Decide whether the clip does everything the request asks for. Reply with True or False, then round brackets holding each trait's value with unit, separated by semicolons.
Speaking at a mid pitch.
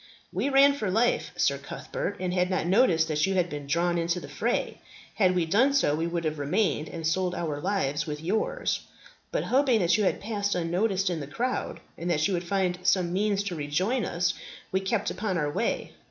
True (180 Hz)